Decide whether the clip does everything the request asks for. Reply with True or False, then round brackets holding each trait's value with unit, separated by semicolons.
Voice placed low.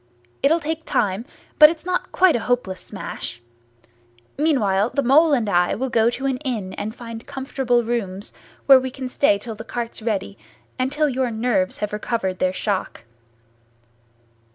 False (240 Hz)